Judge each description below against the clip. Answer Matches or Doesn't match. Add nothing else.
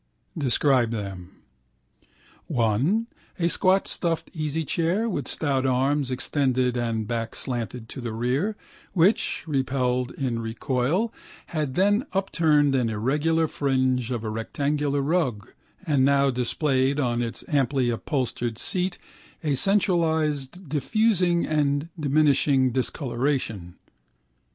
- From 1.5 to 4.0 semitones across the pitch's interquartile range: Doesn't match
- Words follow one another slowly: Matches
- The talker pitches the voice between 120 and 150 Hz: Matches